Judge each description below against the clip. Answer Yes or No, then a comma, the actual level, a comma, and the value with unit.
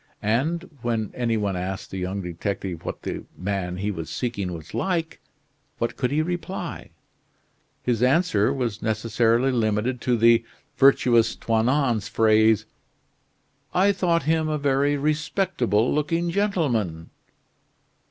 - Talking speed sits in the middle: No, slow, 125 wpm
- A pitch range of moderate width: No, wide, 6.3 semitones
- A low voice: Yes, low, 120 Hz